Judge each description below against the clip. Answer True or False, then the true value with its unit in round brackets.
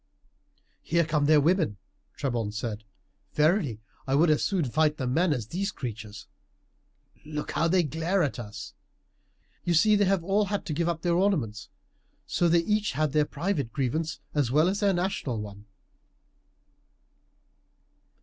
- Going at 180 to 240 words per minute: False (155 wpm)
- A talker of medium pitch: True (155 Hz)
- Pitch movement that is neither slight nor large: False (5.8 semitones)